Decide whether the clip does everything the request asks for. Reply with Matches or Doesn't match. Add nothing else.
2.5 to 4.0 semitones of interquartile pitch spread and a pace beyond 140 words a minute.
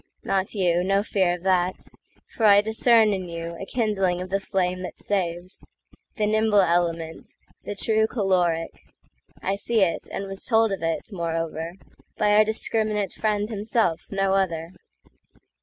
Doesn't match